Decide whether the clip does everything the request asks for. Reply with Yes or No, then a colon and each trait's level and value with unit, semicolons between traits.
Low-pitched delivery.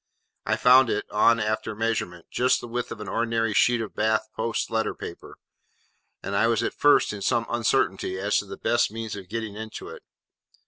Yes: low, 110 Hz